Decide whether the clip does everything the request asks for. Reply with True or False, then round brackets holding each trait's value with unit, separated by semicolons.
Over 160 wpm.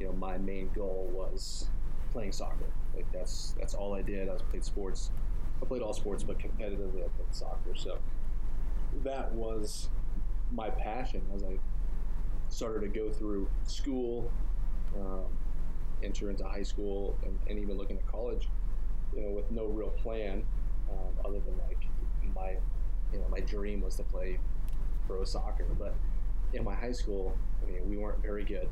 True (170 wpm)